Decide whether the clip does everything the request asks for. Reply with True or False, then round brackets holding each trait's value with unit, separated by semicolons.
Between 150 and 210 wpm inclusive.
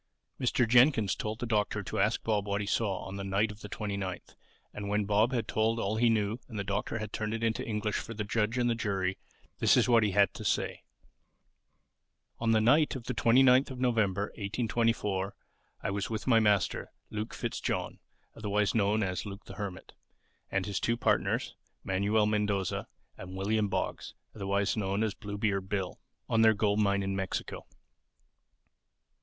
True (180 wpm)